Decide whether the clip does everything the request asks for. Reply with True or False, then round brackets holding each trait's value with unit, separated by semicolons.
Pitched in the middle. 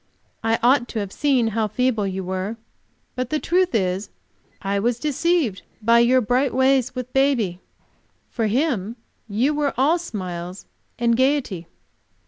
False (235 Hz)